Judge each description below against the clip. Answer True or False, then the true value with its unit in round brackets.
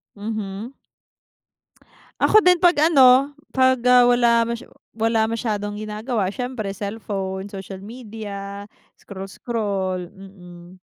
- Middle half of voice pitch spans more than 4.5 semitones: False (3.7 semitones)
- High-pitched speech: True (215 Hz)